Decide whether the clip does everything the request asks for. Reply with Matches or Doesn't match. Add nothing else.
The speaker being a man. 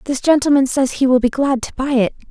Doesn't match